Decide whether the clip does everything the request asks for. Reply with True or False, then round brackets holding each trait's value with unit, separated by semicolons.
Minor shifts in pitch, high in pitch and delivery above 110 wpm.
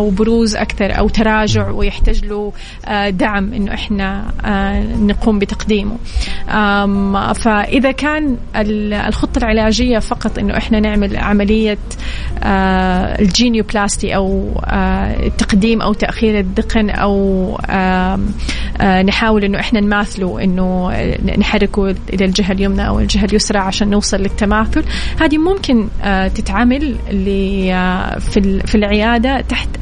False (2.0 semitones; 205 Hz; 105 wpm)